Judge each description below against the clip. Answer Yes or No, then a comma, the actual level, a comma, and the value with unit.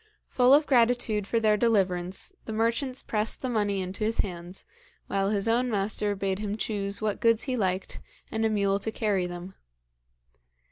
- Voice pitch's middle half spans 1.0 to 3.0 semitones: Yes, average, 2.7 semitones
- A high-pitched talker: Yes, high, 210 Hz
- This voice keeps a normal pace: Yes, average, 175 wpm